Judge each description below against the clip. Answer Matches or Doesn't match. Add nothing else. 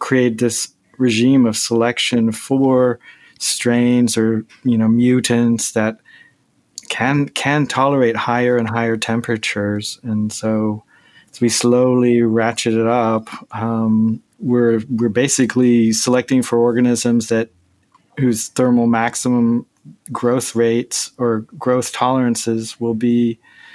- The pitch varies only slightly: Matches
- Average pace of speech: Doesn't match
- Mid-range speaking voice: Doesn't match